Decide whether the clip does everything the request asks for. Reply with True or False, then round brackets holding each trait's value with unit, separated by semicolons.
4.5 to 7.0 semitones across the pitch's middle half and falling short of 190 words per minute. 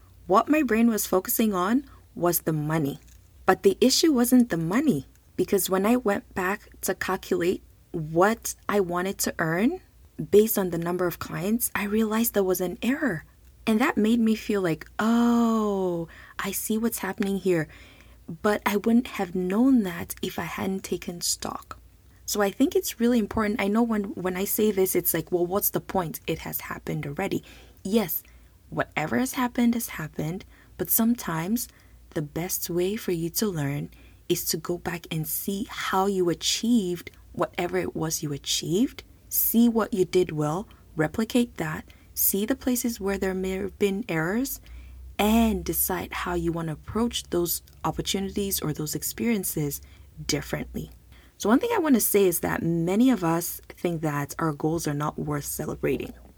True (5.0 semitones; 175 wpm)